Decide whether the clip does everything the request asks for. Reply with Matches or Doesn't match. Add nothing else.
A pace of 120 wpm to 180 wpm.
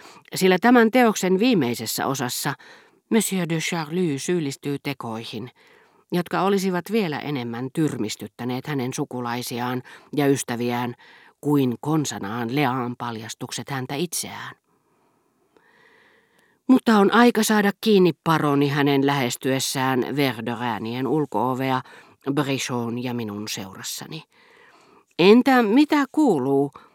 Doesn't match